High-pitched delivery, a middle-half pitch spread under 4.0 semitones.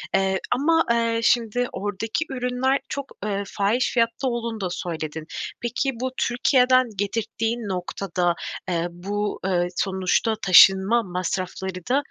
No: high, 210 Hz; average, 4.6 semitones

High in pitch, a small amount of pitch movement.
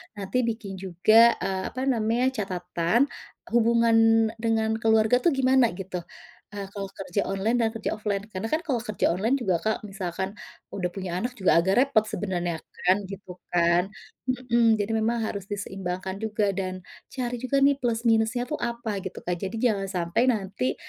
No: high, 215 Hz; average, 3.7 semitones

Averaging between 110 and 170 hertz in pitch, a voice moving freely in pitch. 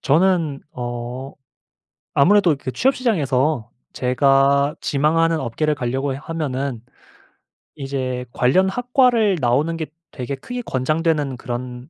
No: medium, 140 Hz; average, 4.4 semitones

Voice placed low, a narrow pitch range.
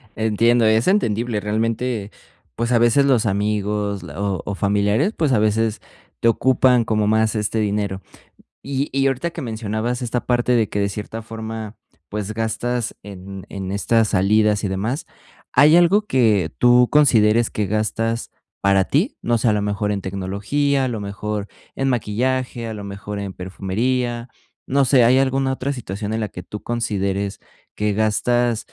No: low, 110 Hz; average, 3.2 semitones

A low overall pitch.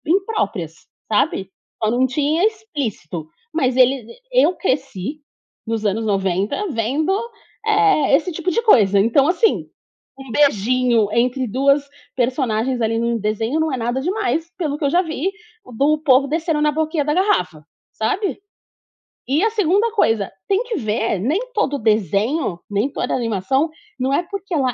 No: very high, 270 Hz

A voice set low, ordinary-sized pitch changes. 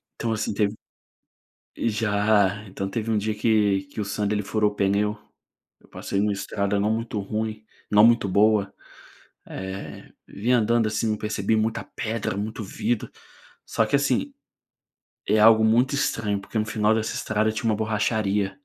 No: low, 105 Hz; narrow, 1.4 semitones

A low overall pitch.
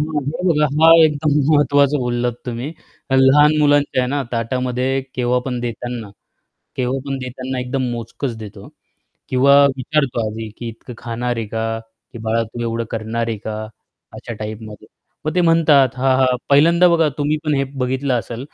Yes: low, 125 Hz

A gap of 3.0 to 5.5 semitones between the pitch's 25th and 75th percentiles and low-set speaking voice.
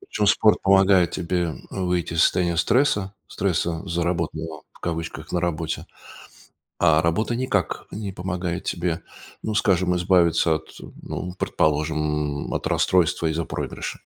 No: narrow, 2.5 semitones; very low, 85 Hz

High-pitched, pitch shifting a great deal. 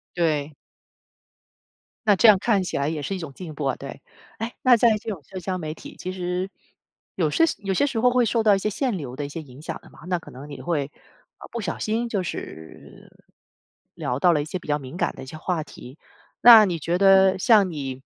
No: medium, 180 Hz; wide, 5.8 semitones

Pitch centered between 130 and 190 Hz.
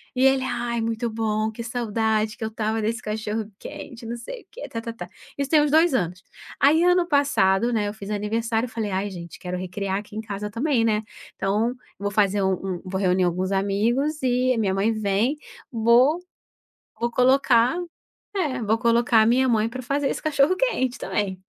No: high, 225 Hz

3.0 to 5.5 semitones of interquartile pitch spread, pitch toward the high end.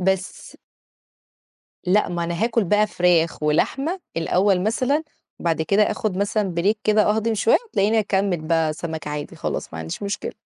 Yes: average, 4.1 semitones; high, 195 Hz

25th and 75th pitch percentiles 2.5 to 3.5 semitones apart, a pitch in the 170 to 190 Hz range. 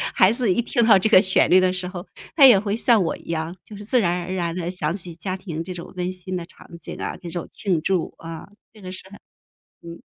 Yes: average, 2.8 semitones; medium, 185 Hz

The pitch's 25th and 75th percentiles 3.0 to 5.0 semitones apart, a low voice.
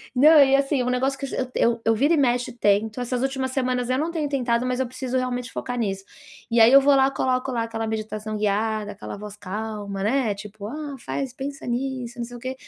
No: average, 3.3 semitones; very high, 250 Hz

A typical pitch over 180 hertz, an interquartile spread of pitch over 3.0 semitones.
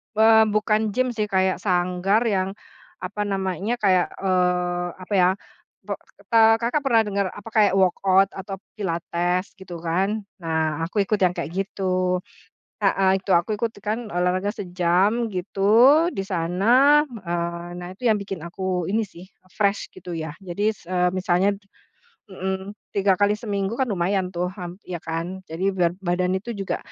No: high, 190 Hz; average, 2.7 semitones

